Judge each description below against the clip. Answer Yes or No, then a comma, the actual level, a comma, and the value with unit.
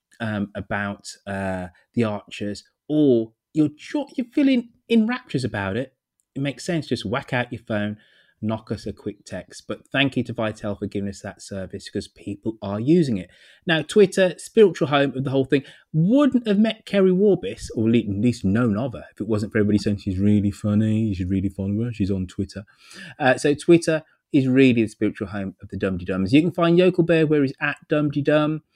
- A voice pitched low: Yes, low, 120 Hz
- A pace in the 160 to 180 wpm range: No, fast, 205 wpm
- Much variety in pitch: Yes, wide, 7.2 semitones